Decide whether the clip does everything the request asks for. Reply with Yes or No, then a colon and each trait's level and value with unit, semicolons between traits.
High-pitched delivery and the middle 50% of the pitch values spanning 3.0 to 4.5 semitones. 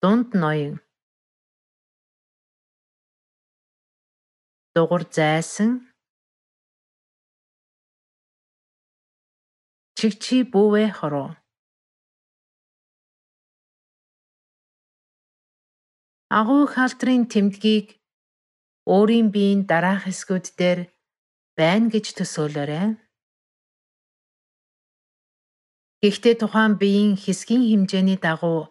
Yes: high, 200 Hz; average, 4.0 semitones